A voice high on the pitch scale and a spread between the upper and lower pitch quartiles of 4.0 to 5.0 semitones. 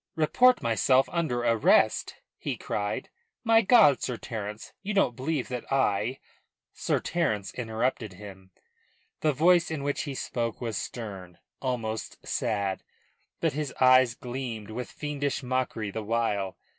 No: low, 125 Hz; average, 4.7 semitones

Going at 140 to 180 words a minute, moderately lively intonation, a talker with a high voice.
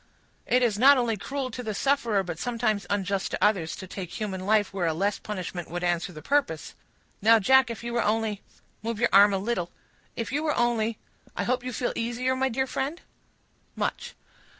No: average, 190 wpm; average, 4.1 semitones; high, 220 Hz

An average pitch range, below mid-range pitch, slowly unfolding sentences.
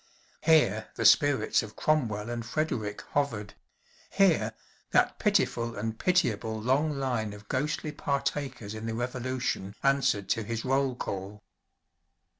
Yes: average, 4.4 semitones; low, 120 Hz; slow, 125 wpm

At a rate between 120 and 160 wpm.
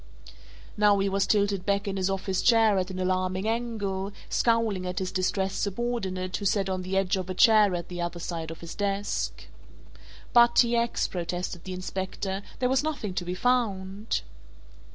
No: average, 180 wpm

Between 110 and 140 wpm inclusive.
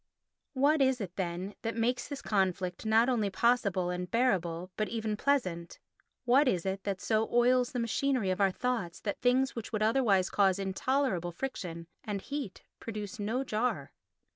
No: average, 165 wpm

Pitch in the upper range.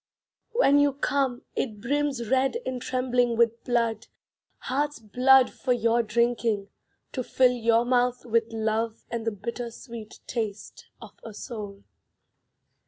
Yes: high, 235 Hz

